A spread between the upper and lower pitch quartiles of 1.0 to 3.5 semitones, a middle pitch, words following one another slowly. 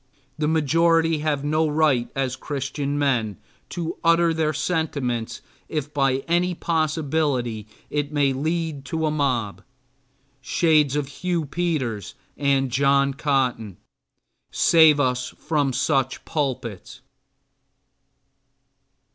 Yes: average, 3.2 semitones; medium, 145 Hz; slow, 110 wpm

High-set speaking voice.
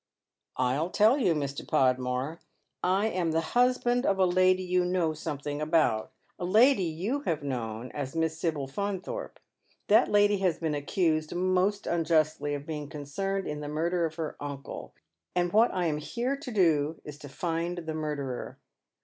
No: medium, 165 Hz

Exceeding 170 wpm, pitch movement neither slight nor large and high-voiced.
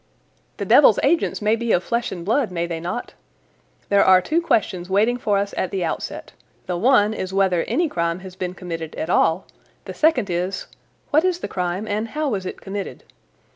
Yes: average, 200 wpm; average, 4.6 semitones; high, 195 Hz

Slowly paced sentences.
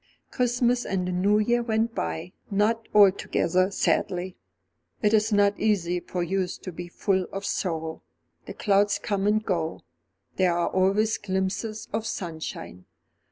No: average, 145 wpm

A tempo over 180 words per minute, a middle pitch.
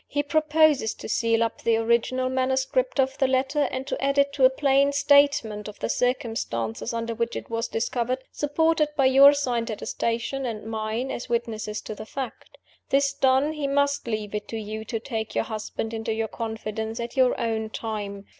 No: average, 190 wpm; high, 240 Hz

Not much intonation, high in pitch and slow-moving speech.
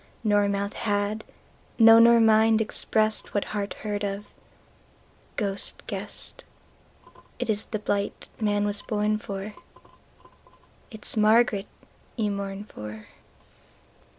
Yes: narrow, 1.3 semitones; high, 210 Hz; slow, 100 wpm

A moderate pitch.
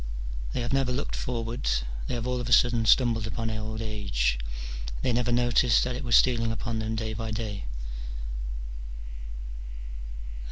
No: low, 115 Hz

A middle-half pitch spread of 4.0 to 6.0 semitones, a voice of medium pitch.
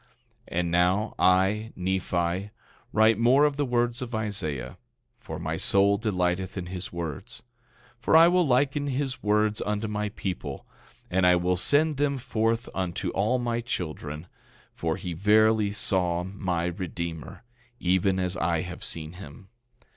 No: average, 4.3 semitones; very low, 95 Hz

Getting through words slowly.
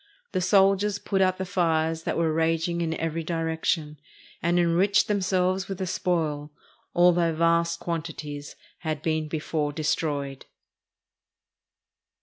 Yes: slow, 125 wpm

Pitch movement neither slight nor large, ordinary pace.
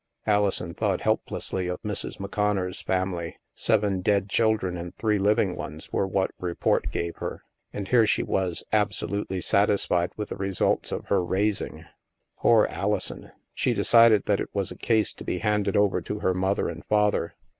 No: narrow, 2.2 semitones; average, 175 wpm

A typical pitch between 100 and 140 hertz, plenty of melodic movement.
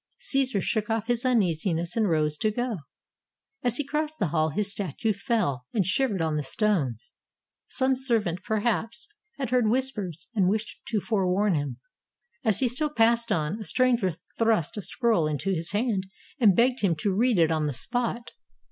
No: high, 210 Hz; wide, 5.8 semitones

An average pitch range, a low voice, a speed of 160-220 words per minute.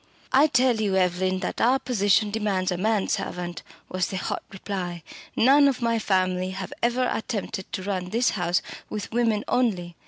No: average, 4.1 semitones; high, 200 Hz; average, 175 wpm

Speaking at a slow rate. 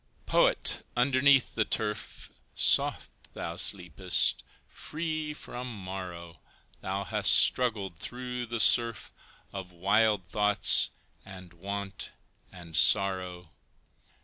Yes: slow, 95 wpm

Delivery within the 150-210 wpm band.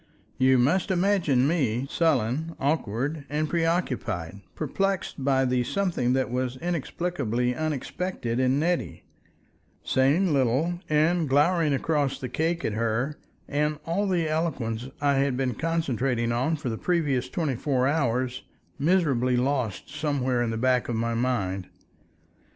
No: slow, 135 wpm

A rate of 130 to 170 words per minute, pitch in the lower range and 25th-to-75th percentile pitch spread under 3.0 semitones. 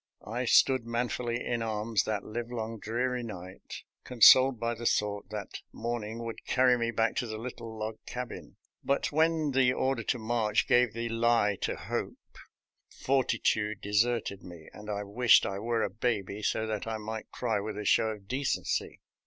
No: average, 180 wpm; low, 115 Hz; narrow, 2.4 semitones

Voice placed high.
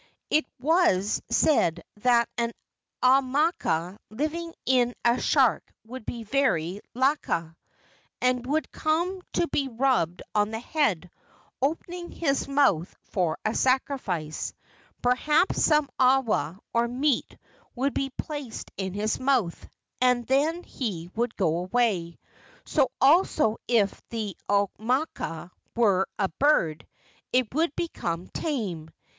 Yes: high, 245 Hz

